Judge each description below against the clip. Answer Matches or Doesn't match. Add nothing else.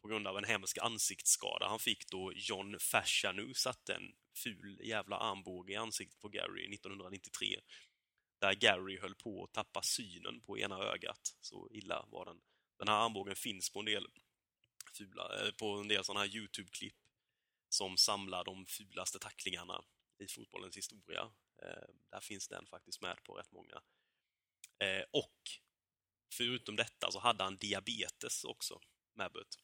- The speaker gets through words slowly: Doesn't match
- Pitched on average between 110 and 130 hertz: Doesn't match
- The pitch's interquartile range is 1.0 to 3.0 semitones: Matches